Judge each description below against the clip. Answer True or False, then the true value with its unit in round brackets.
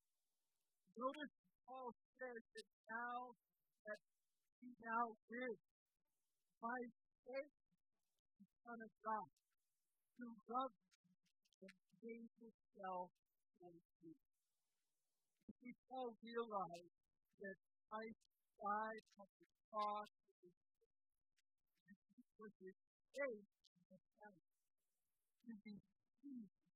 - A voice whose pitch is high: True (215 Hz)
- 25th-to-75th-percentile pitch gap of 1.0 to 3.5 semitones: False (4.1 semitones)